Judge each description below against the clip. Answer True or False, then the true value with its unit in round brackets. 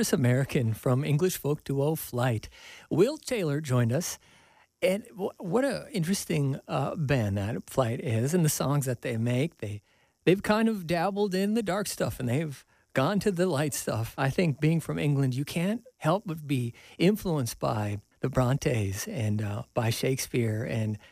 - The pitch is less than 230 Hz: True (140 Hz)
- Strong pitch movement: True (6.7 semitones)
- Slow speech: False (175 wpm)